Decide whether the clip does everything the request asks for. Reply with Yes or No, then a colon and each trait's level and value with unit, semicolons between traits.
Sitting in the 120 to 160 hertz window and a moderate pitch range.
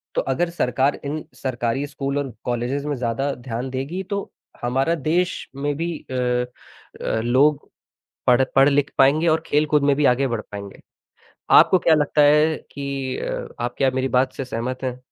Yes: low, 135 Hz; average, 3.0 semitones